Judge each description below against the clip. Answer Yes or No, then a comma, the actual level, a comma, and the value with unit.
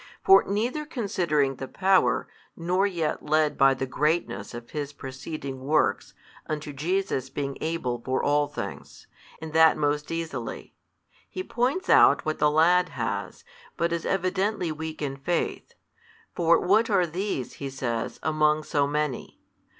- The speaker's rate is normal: Yes, average, 145 wpm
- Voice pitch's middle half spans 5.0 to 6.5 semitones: No, average, 4.2 semitones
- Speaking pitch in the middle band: Yes, medium, 155 Hz